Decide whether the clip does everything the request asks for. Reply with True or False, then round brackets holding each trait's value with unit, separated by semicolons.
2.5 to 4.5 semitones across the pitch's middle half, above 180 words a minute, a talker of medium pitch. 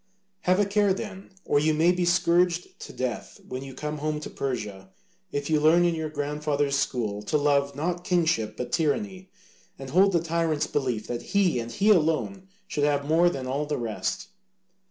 True (4.2 semitones; 190 wpm; 150 Hz)